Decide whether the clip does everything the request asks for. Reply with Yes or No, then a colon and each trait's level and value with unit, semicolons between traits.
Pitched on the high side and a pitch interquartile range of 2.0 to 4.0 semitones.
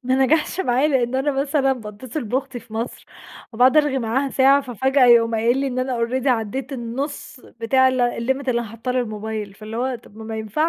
Yes: very high, 250 Hz; average, 2.7 semitones